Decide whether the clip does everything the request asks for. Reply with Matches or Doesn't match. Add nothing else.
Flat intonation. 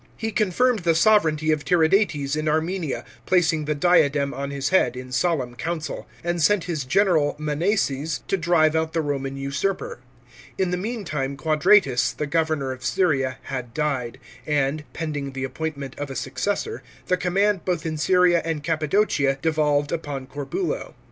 Doesn't match